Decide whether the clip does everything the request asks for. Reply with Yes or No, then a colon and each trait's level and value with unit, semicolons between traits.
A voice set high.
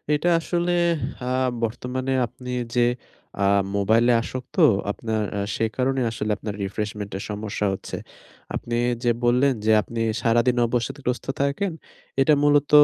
No: low, 120 Hz